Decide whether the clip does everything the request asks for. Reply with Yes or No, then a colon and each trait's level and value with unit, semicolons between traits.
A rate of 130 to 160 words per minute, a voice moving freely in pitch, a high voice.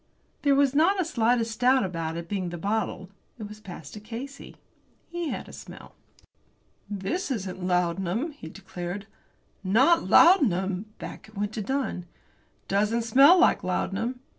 Yes: average, 155 wpm; wide, 6.1 semitones; high, 215 Hz